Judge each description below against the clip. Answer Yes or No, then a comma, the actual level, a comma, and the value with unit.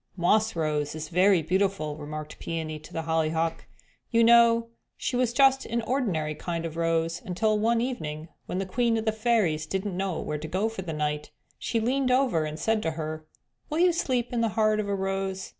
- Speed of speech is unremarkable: No, fast, 210 wpm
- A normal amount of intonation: No, wide, 6.4 semitones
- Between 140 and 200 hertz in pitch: Yes, high, 190 Hz